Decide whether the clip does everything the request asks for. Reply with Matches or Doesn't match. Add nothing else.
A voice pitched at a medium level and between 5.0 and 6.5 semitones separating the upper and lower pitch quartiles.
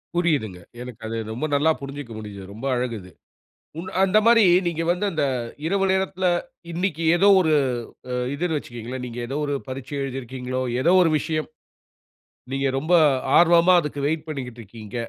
Matches